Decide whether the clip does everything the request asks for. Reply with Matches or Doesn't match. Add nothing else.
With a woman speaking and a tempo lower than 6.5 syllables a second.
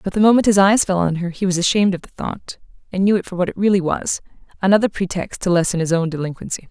Doesn't match